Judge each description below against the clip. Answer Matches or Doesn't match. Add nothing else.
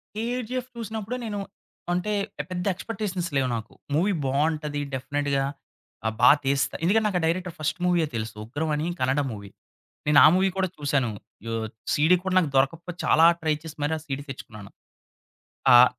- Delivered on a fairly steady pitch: Doesn't match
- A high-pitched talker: Doesn't match